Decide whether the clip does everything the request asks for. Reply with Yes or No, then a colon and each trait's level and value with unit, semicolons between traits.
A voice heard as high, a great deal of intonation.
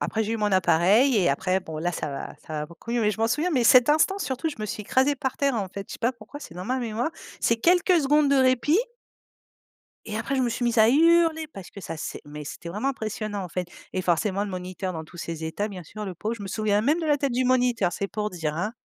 Yes: high, 215 Hz; wide, 6.0 semitones